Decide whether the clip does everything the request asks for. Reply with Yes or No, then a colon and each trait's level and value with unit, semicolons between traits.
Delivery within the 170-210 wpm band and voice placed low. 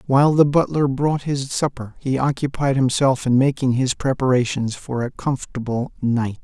No: average, 160 wpm; low, 130 Hz